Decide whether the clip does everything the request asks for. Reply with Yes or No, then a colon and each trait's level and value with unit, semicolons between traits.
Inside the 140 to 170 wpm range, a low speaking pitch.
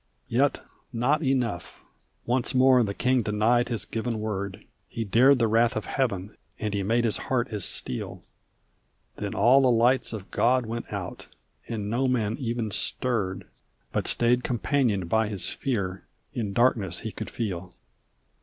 Yes: average, 155 wpm; low, 115 Hz